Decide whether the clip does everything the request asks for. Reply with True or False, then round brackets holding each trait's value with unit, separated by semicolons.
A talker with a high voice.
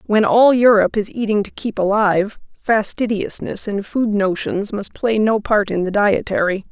True (210 Hz)